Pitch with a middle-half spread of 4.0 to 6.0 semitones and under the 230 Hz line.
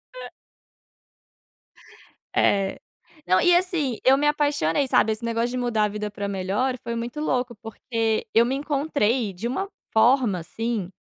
No: average, 4.3 semitones; high, 235 Hz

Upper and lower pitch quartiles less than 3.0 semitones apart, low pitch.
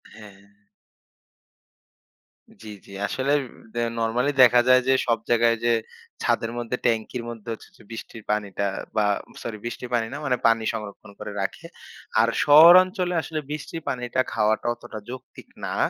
Yes: narrow, 2.6 semitones; low, 120 Hz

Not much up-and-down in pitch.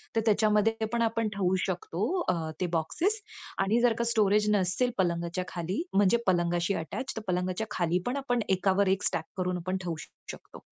No: average, 3.7 semitones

